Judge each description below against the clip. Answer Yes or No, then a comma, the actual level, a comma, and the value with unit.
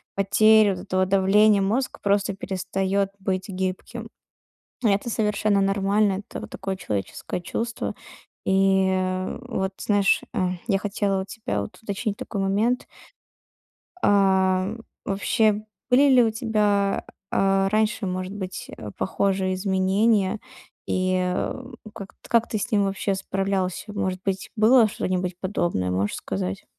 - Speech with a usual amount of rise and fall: No, narrow, 2.0 semitones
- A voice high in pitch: Yes, high, 195 Hz